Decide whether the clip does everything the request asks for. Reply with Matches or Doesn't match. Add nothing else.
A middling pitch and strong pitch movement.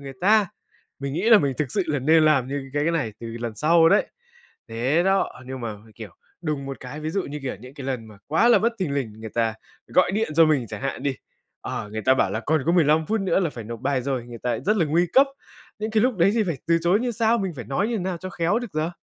Matches